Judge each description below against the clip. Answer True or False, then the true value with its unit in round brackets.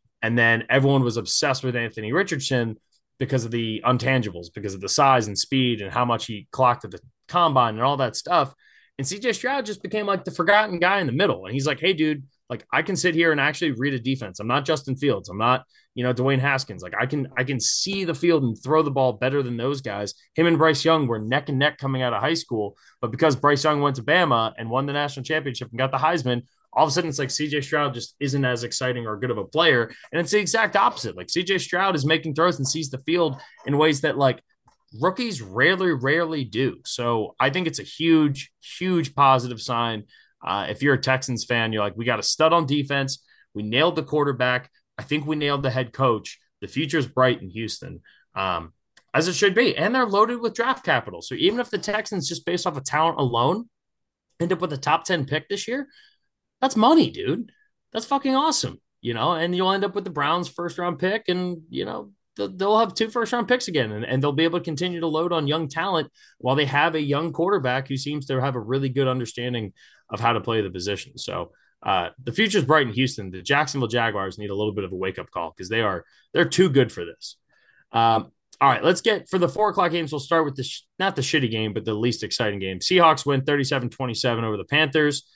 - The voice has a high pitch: False (140 Hz)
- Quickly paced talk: True (240 wpm)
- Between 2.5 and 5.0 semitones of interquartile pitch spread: False (5.6 semitones)